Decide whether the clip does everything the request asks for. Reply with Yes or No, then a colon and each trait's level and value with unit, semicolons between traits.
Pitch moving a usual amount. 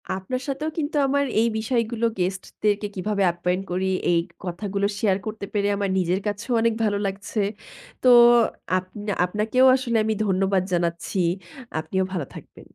Yes: average, 3.1 semitones